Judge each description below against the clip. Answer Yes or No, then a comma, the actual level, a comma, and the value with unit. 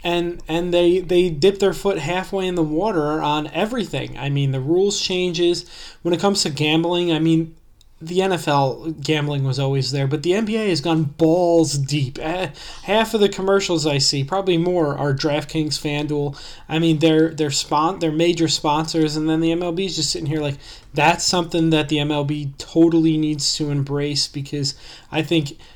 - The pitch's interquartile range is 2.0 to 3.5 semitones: Yes, average, 2.9 semitones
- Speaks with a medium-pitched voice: Yes, medium, 160 Hz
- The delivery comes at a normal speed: Yes, average, 180 wpm